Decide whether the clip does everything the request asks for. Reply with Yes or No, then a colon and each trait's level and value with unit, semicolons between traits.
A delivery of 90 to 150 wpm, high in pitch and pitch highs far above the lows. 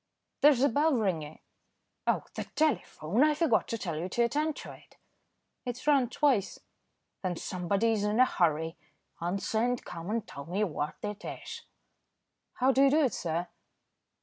No: average, 170 wpm; high, 220 Hz; wide, 7.1 semitones